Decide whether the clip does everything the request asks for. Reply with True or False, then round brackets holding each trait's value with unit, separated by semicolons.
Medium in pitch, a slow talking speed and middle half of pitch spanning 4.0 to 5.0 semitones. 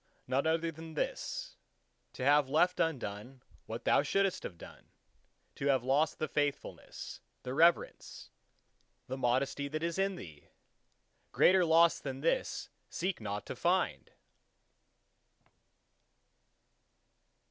True (150 Hz; 115 wpm; 4.3 semitones)